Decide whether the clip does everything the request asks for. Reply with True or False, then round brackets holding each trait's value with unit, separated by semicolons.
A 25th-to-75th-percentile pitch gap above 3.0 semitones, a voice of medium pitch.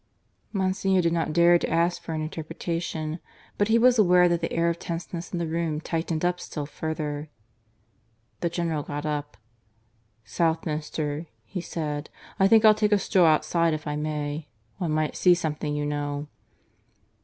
False (2.5 semitones; 165 Hz)